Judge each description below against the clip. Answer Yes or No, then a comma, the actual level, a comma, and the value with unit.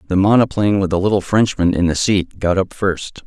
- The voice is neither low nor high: No, very low, 95 Hz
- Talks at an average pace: No, fast, 220 wpm